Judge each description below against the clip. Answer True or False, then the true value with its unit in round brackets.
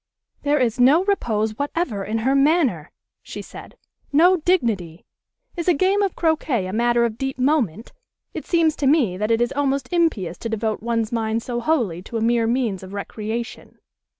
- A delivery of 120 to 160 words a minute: False (180 wpm)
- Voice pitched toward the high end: True (240 Hz)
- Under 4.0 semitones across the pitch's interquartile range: False (5.4 semitones)